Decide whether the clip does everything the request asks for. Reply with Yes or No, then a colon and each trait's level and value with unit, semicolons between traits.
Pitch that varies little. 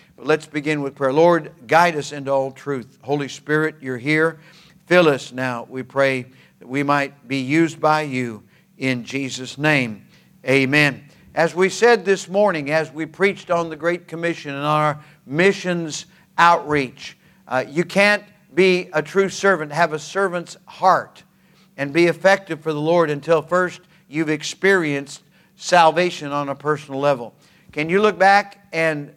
No: average, 3.9 semitones